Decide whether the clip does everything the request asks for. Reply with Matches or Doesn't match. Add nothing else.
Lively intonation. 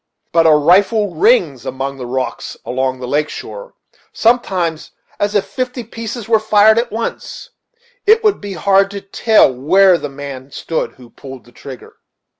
Matches